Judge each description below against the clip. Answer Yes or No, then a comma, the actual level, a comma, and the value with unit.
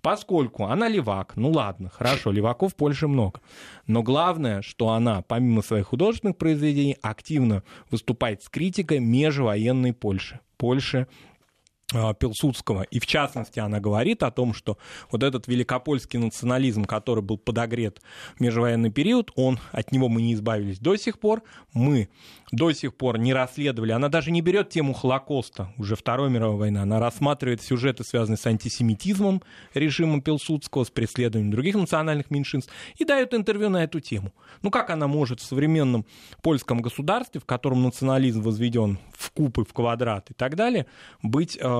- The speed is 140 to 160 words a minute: Yes, average, 155 wpm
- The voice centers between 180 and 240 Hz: No, low, 125 Hz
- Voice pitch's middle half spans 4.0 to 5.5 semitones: Yes, average, 4.8 semitones